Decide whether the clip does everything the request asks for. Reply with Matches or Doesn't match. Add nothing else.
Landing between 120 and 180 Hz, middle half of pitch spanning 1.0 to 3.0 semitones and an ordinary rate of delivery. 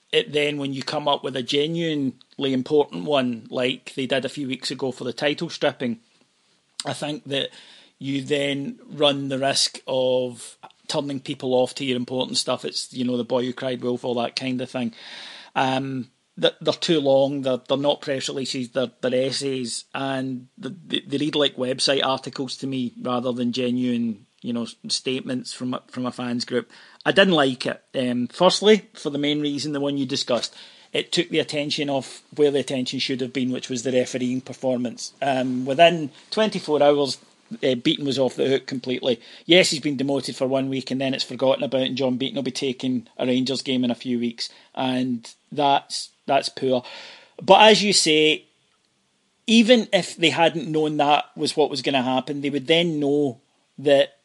Matches